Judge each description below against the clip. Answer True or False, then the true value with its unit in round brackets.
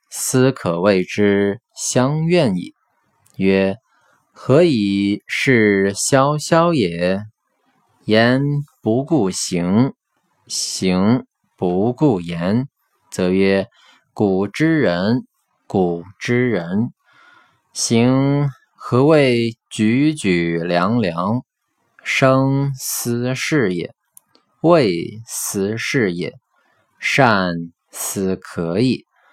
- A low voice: True (110 Hz)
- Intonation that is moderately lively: False (5.7 semitones)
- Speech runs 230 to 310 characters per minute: False (100 characters per minute)